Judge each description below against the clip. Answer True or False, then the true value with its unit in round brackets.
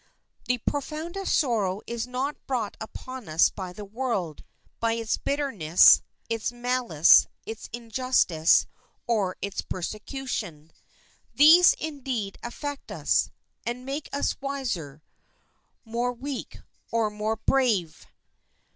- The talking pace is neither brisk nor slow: False (110 wpm)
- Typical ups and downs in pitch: True (5.0 semitones)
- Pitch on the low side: False (235 Hz)